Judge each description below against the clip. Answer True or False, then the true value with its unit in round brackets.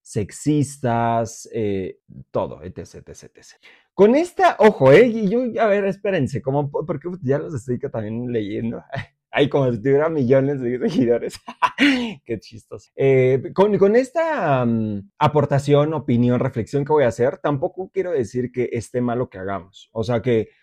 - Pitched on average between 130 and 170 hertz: True (135 Hz)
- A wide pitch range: True (7.1 semitones)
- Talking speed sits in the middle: True (165 wpm)